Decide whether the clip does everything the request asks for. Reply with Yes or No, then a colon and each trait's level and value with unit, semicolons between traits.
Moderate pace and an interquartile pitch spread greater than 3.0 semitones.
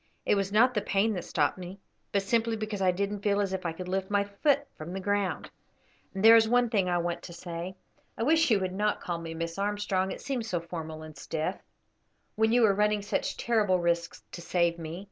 No: fast, 230 wpm; average, 3.4 semitones